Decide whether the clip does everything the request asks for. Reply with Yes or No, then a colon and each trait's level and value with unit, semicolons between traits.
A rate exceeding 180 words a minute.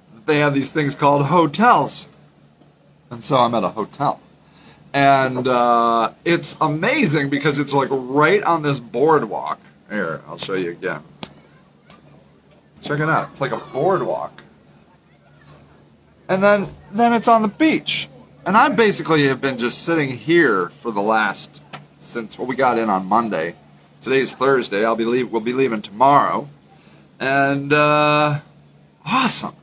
No: average, 145 wpm